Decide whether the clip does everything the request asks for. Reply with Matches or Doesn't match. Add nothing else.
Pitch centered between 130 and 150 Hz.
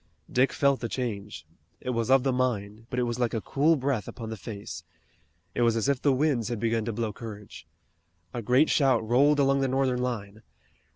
Doesn't match